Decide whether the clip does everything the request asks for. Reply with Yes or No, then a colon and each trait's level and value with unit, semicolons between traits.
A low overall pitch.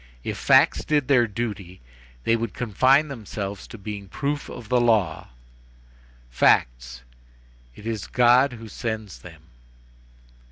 Yes: low, 110 Hz